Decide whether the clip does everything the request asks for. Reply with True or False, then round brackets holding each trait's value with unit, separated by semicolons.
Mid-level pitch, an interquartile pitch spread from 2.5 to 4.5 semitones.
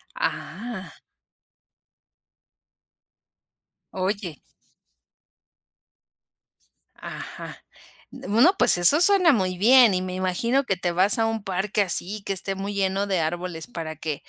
False (195 Hz; 3.7 semitones)